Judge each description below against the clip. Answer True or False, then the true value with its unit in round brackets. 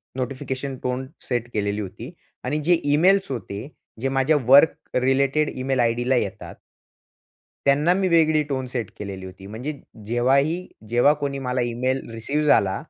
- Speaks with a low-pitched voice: True (130 Hz)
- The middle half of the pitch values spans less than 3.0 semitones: False (3.3 semitones)